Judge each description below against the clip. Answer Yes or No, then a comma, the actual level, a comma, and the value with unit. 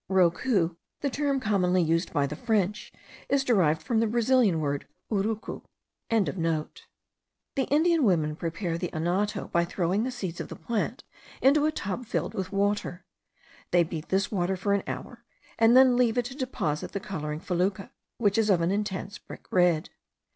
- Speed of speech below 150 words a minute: No, average, 170 wpm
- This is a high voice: Yes, high, 195 Hz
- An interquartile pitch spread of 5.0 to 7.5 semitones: Yes, average, 5.3 semitones